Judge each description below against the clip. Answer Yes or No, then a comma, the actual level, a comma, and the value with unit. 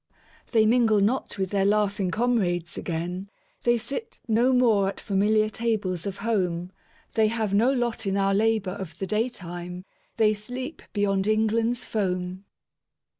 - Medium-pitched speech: No, high, 210 Hz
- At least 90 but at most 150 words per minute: Yes, slow, 135 wpm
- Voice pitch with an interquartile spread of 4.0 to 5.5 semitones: No, average, 3.0 semitones